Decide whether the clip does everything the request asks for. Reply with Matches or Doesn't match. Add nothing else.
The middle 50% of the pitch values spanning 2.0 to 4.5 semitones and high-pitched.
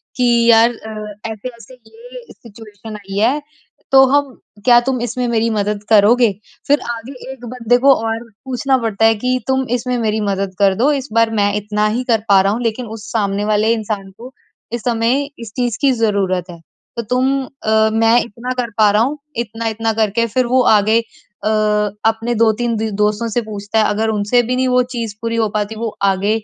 Matches